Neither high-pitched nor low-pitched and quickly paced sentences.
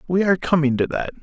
Yes: medium, 160 Hz; fast, 245 wpm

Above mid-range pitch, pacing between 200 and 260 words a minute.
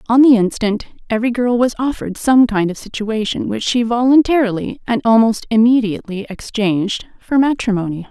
No: high, 225 Hz; average, 150 wpm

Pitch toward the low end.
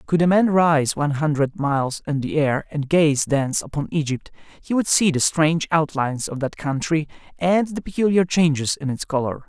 No: medium, 155 Hz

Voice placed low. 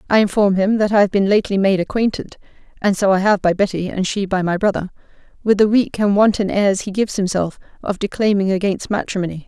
No: high, 195 Hz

